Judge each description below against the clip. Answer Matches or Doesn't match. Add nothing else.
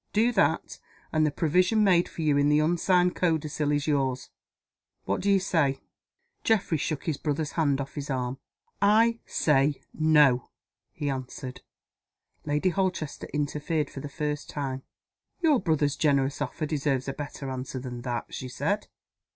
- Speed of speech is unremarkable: Matches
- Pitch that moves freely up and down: Doesn't match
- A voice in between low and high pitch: Matches